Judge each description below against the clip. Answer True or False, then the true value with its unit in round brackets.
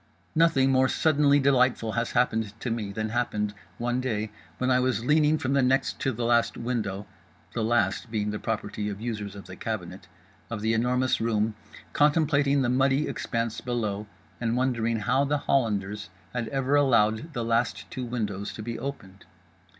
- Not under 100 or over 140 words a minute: False (165 wpm)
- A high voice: False (120 Hz)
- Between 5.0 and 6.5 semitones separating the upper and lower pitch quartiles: False (3.6 semitones)